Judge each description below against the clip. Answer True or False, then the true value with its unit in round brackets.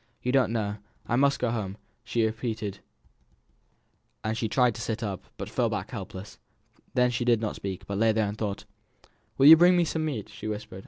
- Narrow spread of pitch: False (3.0 semitones)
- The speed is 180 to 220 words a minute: True (200 wpm)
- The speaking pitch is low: True (110 Hz)